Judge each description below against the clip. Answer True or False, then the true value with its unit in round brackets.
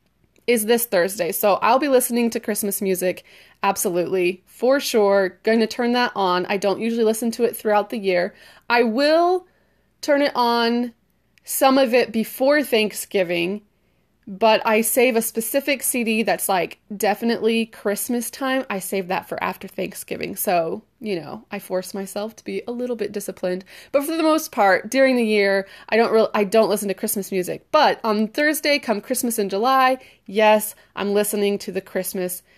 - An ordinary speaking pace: True (175 wpm)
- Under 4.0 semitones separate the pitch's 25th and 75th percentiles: True (3.6 semitones)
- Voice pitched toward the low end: False (220 Hz)